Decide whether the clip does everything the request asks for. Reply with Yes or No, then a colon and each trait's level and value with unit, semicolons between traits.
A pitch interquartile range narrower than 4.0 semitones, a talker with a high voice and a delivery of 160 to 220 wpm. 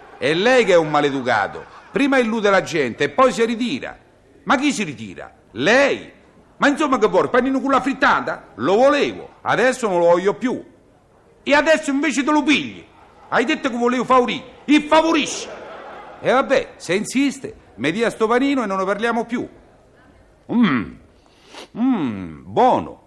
No: average, 4.5 semitones; very high, 255 Hz; average, 165 wpm